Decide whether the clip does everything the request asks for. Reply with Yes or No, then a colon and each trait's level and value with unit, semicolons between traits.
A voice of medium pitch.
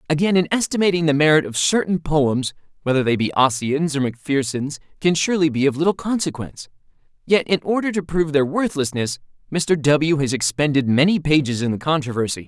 Yes: medium, 150 Hz